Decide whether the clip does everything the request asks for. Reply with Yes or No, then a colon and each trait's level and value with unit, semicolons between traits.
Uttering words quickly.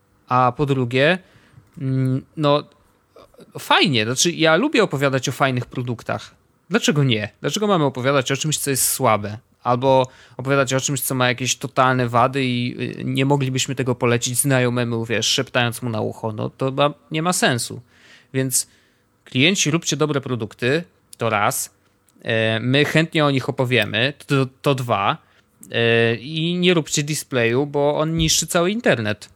No: average, 145 wpm